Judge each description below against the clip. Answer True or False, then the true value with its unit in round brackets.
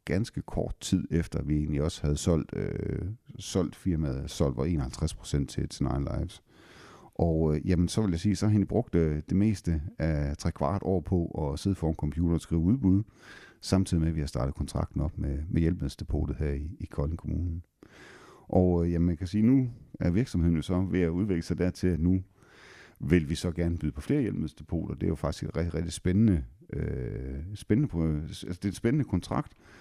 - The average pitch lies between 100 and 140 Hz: False (85 Hz)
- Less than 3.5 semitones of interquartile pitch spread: False (3.8 semitones)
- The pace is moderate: True (195 wpm)